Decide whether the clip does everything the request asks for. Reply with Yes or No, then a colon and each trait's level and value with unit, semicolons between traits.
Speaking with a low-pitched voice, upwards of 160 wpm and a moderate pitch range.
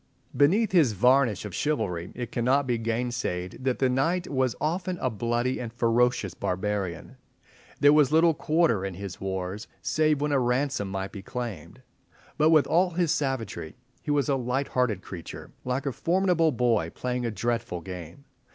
No: low, 125 Hz; average, 170 wpm; wide, 5.9 semitones